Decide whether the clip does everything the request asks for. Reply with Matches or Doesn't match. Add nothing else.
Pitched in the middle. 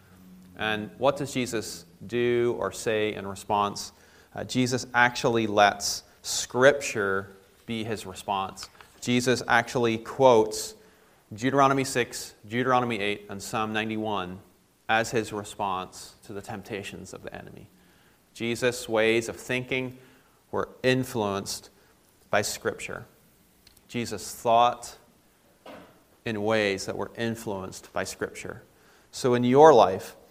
Doesn't match